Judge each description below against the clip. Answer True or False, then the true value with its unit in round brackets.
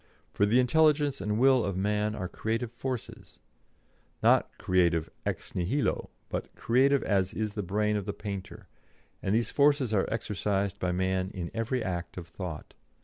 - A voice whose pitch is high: False (105 Hz)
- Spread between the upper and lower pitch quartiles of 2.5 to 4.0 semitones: False (4.4 semitones)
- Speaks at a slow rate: False (160 wpm)